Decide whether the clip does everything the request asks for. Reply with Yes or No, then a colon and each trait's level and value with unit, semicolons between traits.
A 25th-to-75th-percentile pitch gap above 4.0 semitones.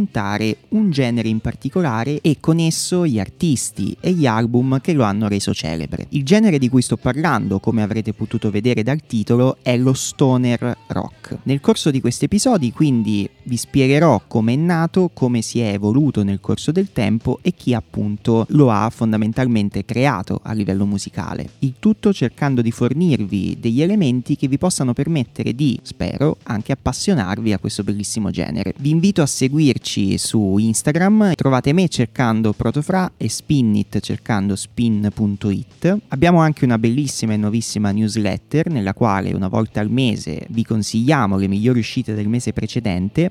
Yes: average, 5.1 semitones